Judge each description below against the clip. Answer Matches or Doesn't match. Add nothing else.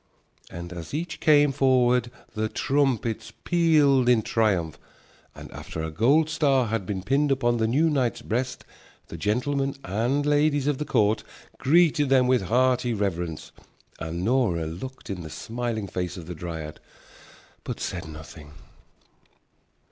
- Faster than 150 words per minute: Doesn't match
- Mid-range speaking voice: Doesn't match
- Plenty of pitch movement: Matches